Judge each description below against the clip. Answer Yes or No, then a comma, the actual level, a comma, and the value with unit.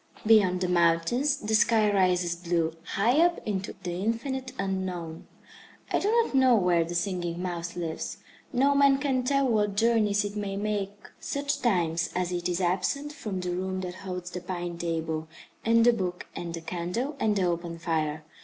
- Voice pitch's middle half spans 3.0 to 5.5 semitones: Yes, average, 4.7 semitones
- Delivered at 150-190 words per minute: Yes, average, 180 wpm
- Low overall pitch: No, medium, 185 Hz